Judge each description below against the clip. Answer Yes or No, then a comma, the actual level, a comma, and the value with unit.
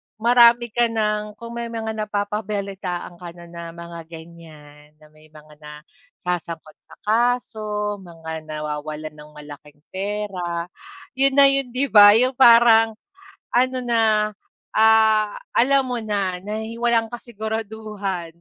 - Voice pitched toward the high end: Yes, high, 210 Hz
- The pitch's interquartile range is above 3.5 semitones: Yes, average, 5.2 semitones